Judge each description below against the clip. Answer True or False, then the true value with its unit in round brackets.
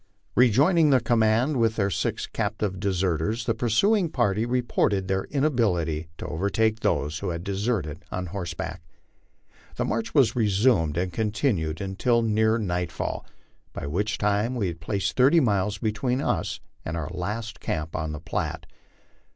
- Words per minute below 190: True (150 wpm)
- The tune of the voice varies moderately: True (4.7 semitones)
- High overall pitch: False (105 Hz)